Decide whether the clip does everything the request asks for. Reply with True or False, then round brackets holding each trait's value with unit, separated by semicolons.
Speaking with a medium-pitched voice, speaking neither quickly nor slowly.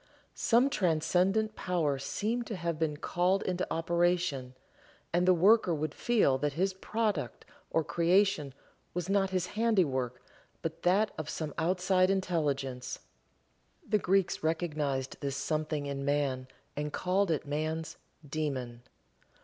False (165 Hz; 130 wpm)